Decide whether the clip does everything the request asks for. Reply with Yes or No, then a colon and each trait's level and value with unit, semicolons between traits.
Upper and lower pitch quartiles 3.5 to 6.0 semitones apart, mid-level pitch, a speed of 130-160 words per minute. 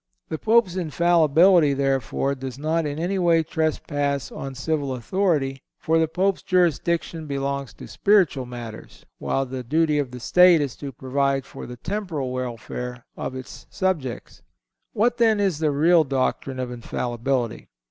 Yes: average, 4.5 semitones; medium, 145 Hz; average, 150 wpm